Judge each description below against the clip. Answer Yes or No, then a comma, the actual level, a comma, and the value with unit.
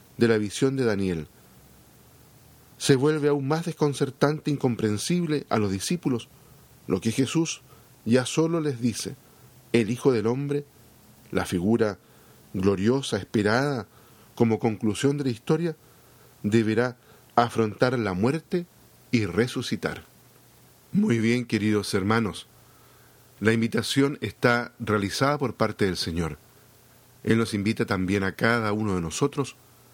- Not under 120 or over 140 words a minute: Yes, slow, 125 wpm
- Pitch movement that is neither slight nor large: Yes, average, 4.3 semitones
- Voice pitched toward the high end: No, low, 115 Hz